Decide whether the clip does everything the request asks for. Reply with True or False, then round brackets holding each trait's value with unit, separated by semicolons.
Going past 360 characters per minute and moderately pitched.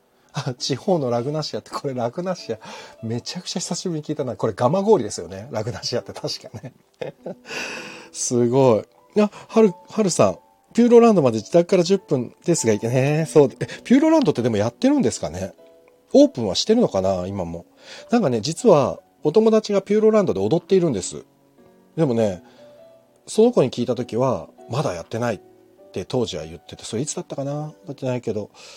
True (390 characters per minute; 145 Hz)